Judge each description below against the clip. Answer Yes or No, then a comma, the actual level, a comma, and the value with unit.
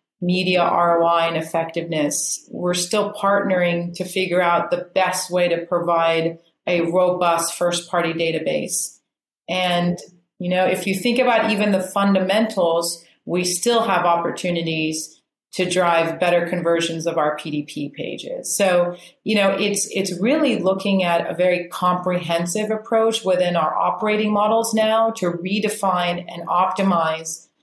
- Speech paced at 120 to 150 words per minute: Yes, slow, 135 wpm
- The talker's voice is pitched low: No, medium, 180 Hz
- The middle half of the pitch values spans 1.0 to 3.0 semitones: Yes, narrow, 2.5 semitones